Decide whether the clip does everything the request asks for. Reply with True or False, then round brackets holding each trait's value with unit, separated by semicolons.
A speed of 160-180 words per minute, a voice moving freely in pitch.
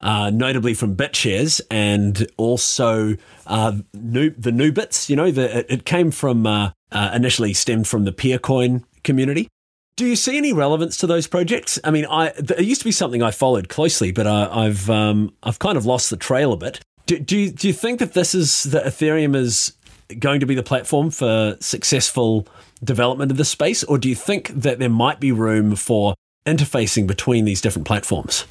False (200 wpm; 5.8 semitones)